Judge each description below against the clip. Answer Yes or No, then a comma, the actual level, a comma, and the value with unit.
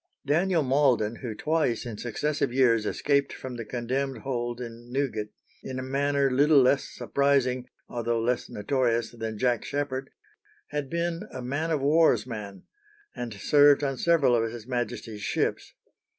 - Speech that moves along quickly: No, average, 150 wpm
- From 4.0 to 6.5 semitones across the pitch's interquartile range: No, average, 3.2 semitones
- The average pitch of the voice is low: Yes, low, 130 Hz